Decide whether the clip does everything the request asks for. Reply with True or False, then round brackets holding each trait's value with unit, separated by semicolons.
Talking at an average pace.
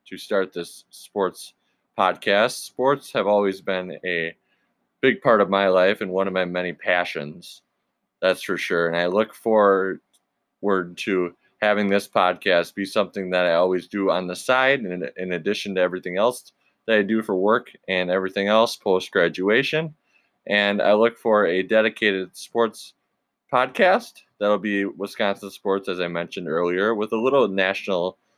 True (165 wpm)